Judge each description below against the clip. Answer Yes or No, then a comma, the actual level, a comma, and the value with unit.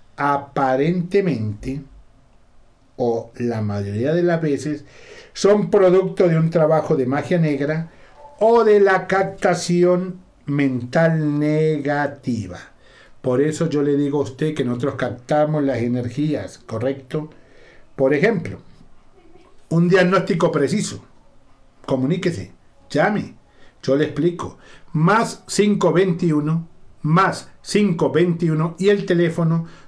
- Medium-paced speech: No, slow, 100 wpm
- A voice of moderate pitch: Yes, medium, 155 Hz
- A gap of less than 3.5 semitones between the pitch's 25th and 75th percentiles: No, average, 4.6 semitones